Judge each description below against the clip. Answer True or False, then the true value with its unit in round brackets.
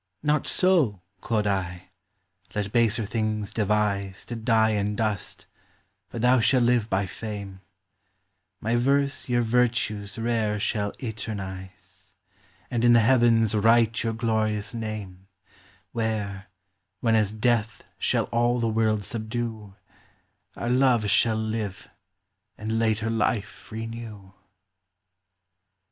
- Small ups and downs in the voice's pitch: True (2.3 semitones)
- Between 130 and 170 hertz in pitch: False (110 Hz)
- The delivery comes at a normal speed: False (115 wpm)